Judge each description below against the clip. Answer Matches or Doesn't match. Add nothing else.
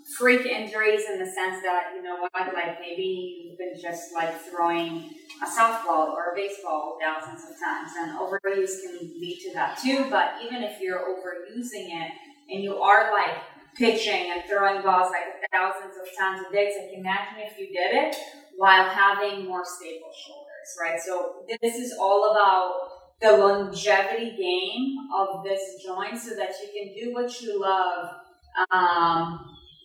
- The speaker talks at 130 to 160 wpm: Doesn't match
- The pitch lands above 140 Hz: Matches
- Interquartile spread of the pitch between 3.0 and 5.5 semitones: Matches